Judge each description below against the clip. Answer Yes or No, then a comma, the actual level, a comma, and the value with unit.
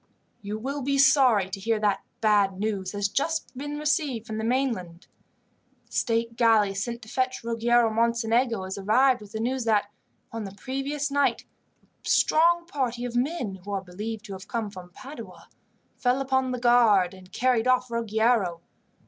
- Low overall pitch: No, high, 230 Hz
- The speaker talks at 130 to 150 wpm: No, average, 175 wpm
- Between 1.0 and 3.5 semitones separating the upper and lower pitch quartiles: No, average, 3.9 semitones